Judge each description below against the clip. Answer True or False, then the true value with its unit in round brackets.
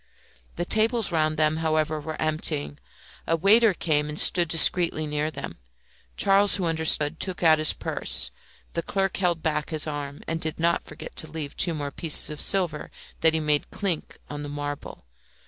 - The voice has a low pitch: False (160 Hz)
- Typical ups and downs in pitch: False (2.3 semitones)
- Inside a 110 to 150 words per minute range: False (180 wpm)